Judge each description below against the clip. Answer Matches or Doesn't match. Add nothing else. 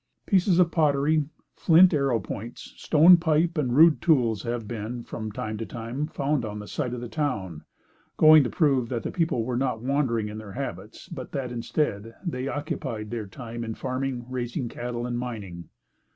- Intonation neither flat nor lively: Matches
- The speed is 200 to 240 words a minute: Doesn't match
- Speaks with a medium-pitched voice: Doesn't match